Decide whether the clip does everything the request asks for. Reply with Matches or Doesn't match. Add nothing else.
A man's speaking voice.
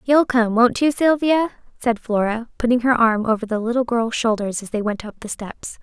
Doesn't match